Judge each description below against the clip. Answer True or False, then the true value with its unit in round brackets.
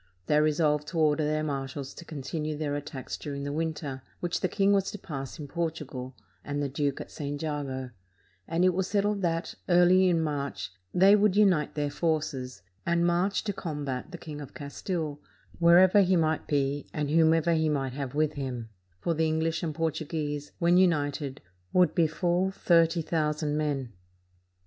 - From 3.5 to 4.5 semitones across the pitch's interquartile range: False (3.0 semitones)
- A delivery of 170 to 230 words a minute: True (180 wpm)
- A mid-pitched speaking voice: True (155 Hz)